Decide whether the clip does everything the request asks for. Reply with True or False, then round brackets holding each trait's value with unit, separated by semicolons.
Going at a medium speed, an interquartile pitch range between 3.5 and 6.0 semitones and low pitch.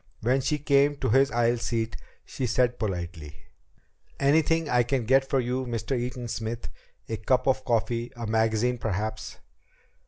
False (155 wpm; 2.9 semitones; 120 Hz)